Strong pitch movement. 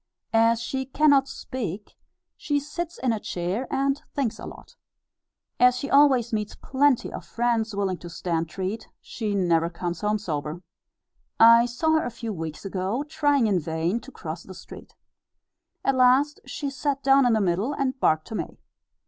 Yes: wide, 6.4 semitones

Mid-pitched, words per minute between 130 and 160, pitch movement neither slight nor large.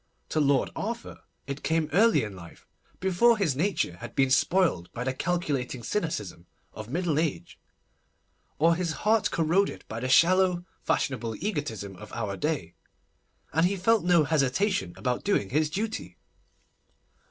No: medium, 155 Hz; average, 140 wpm; wide, 6.6 semitones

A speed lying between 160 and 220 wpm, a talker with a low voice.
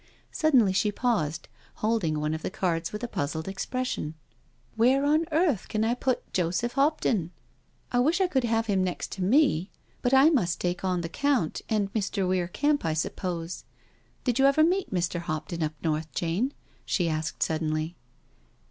No: average, 175 wpm; high, 195 Hz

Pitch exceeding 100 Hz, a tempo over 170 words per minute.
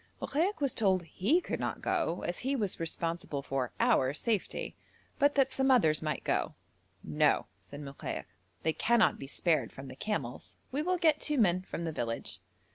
Yes: medium, 185 Hz; average, 180 wpm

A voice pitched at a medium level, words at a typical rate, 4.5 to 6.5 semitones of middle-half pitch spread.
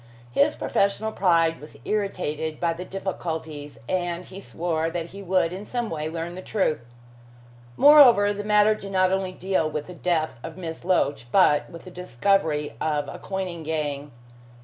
No: medium, 175 Hz; average, 170 wpm; average, 3.6 semitones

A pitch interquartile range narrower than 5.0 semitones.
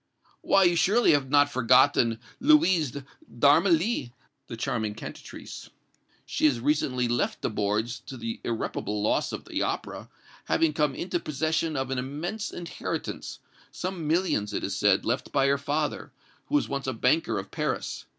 No: wide, 5.6 semitones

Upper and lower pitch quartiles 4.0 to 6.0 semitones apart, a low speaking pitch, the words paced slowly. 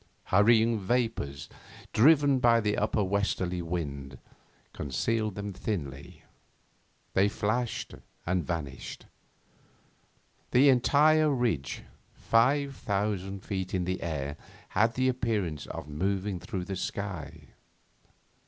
Yes: average, 4.9 semitones; low, 100 Hz; slow, 105 wpm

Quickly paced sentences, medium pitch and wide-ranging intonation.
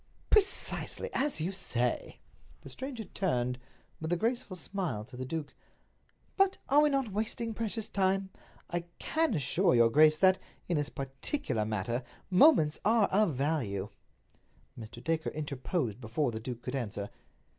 No: average, 145 wpm; medium, 160 Hz; wide, 9.0 semitones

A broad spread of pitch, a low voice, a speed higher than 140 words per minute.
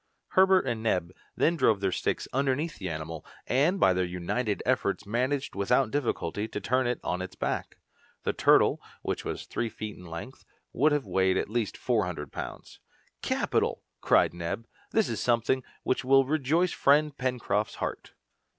Yes: wide, 6.2 semitones; low, 120 Hz; average, 170 wpm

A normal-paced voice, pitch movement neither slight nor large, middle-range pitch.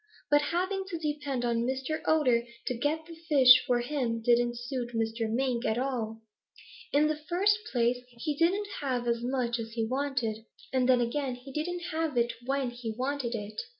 No: average, 185 wpm; average, 3.9 semitones; very high, 255 Hz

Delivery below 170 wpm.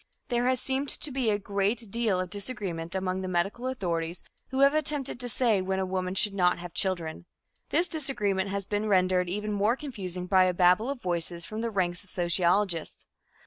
No: average, 195 wpm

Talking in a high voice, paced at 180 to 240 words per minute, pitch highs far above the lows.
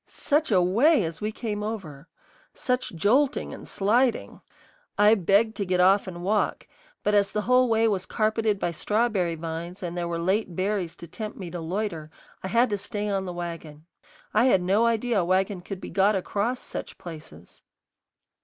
No: high, 200 Hz; average, 185 wpm; average, 3.8 semitones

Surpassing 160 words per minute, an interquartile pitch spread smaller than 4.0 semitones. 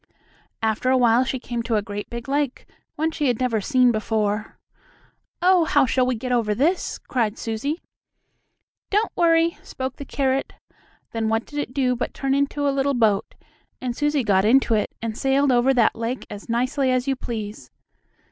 Yes: average, 185 wpm; average, 3.6 semitones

